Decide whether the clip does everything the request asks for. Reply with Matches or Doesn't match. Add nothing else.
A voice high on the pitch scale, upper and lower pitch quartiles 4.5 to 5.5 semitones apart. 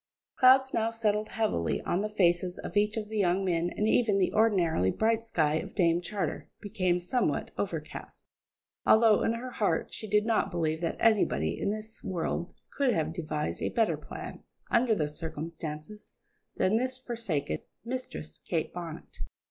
Matches